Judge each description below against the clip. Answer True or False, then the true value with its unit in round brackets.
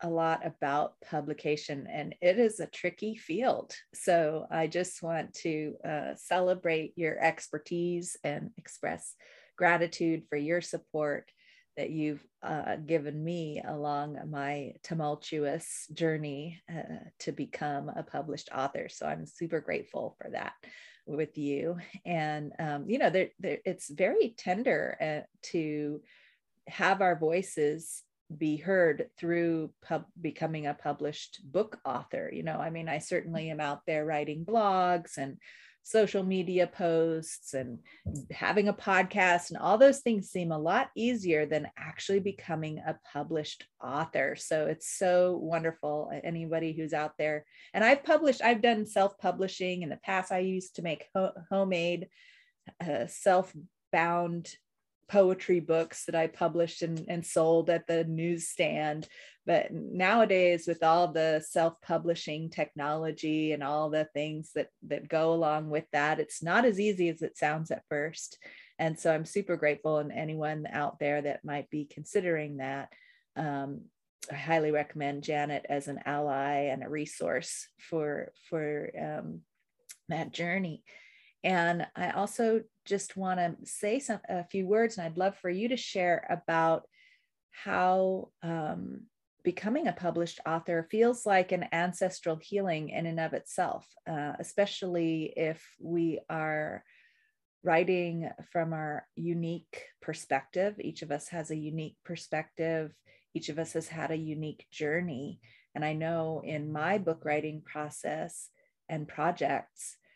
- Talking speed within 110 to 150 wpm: True (145 wpm)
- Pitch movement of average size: True (3.3 semitones)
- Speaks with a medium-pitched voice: True (165 Hz)